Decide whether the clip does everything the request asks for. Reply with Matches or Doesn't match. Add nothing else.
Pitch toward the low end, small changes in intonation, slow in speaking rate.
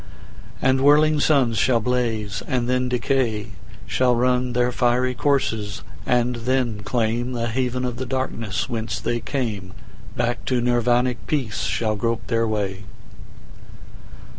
Matches